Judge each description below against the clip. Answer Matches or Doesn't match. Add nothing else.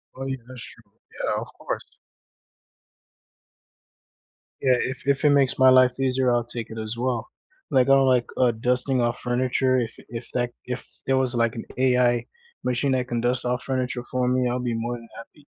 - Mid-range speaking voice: Doesn't match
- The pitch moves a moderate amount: Doesn't match